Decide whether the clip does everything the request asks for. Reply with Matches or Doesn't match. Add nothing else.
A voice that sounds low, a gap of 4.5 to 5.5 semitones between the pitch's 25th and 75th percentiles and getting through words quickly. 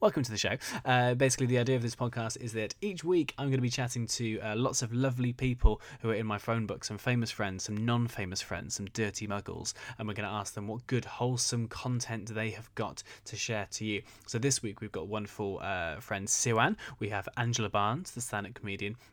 Doesn't match